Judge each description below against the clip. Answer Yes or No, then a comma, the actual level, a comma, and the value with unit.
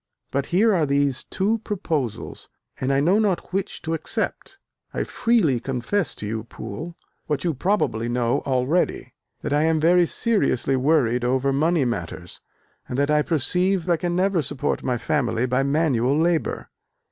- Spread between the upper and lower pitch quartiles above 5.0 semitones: Yes, wide, 5.6 semitones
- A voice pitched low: No, medium, 150 Hz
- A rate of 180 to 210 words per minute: No, average, 160 wpm